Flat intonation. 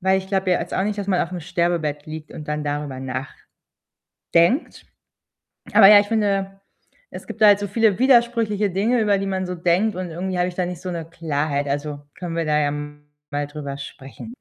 No: average, 4.9 semitones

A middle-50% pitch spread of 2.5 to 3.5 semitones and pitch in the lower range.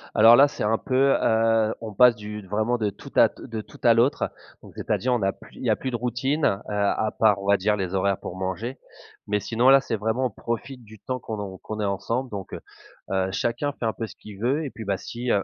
Yes: average, 3.1 semitones; low, 110 Hz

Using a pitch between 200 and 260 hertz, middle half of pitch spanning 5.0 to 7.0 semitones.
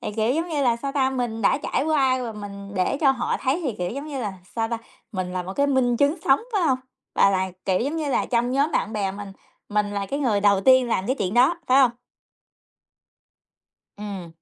Yes: high, 240 Hz; average, 5.3 semitones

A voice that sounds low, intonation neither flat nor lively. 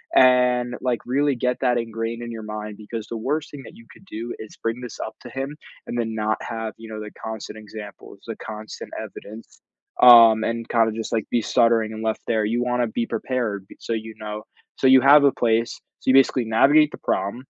No: low, 115 Hz; narrow, 2.2 semitones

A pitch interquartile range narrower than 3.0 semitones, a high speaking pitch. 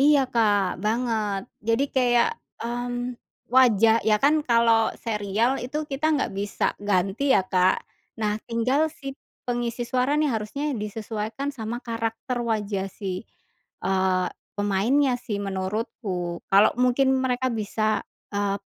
No: average, 3.6 semitones; high, 230 Hz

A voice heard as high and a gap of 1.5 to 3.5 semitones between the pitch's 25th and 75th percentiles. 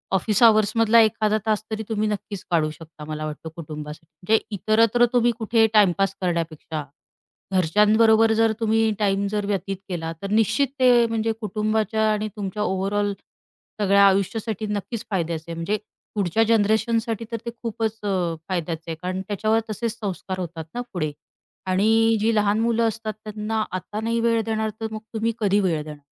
Yes: high, 210 Hz; average, 3.2 semitones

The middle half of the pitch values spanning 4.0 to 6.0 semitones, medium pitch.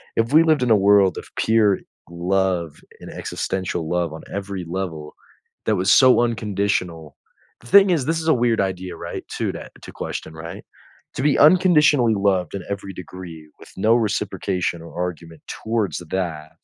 No: average, 5.1 semitones; very low, 95 Hz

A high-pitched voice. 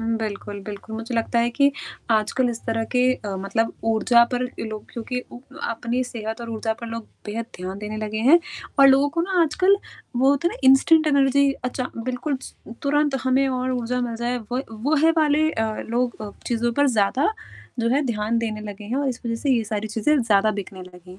Yes: high, 235 Hz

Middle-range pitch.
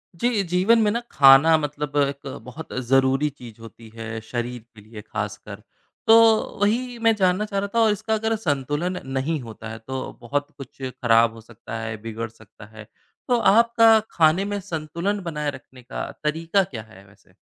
Yes: medium, 145 Hz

